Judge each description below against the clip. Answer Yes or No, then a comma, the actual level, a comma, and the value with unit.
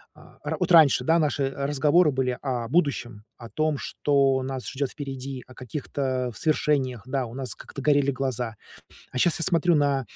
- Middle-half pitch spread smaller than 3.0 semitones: Yes, narrow, 2.5 semitones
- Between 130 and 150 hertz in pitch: Yes, low, 135 Hz